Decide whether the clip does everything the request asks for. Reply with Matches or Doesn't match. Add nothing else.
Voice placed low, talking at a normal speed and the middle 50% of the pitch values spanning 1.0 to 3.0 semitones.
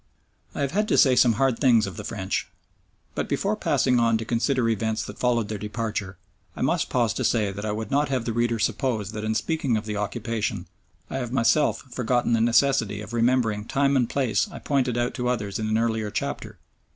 Doesn't match